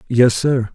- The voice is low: Yes, low, 120 Hz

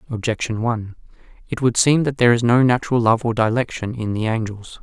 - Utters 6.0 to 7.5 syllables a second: Yes, 6.1 syllables/s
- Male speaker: Yes, male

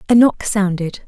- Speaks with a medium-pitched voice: No, high, 200 Hz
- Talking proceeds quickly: No, average, 170 wpm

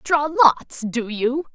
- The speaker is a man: No, female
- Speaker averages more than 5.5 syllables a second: No, 2.9 syllables/s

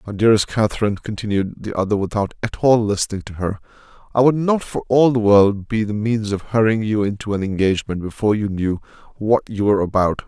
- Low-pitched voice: Yes, low, 105 Hz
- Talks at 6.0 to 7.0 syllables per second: Yes, 6.1 syllables/s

